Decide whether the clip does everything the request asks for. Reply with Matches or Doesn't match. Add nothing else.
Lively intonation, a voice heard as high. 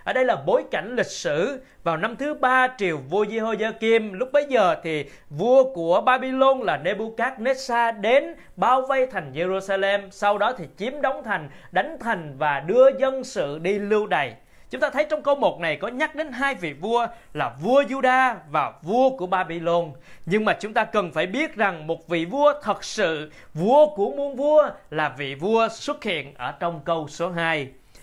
Matches